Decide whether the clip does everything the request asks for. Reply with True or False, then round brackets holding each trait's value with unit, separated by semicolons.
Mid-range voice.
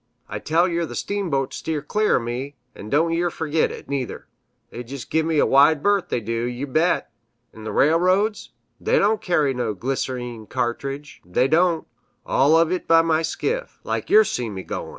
True (150 Hz)